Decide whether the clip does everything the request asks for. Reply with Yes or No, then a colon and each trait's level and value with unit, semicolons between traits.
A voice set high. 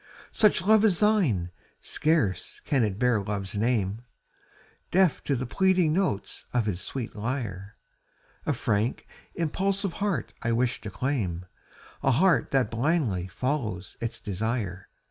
No: low, 120 Hz